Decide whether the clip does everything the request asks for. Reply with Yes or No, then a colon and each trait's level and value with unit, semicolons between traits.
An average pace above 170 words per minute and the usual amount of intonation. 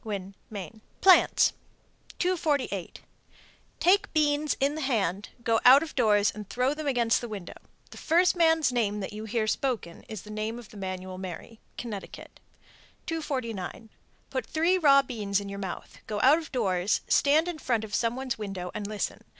No: average, 180 wpm; wide, 6.0 semitones